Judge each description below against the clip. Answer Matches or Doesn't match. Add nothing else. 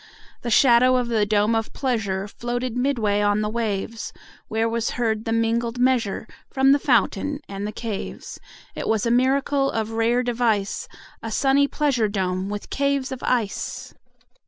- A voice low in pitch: Doesn't match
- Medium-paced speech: Matches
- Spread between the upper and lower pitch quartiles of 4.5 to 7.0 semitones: Doesn't match